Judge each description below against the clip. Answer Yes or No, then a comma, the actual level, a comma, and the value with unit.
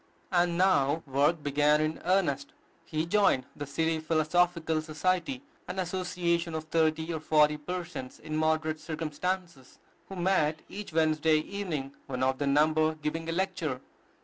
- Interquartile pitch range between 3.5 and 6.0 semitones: No, narrow, 2.6 semitones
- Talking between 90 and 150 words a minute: Yes, average, 145 wpm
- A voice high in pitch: No, medium, 160 Hz